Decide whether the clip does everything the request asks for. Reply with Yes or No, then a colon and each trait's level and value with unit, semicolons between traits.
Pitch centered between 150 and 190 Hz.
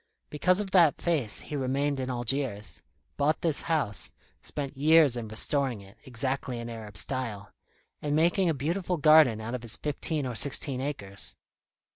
No: low, 135 Hz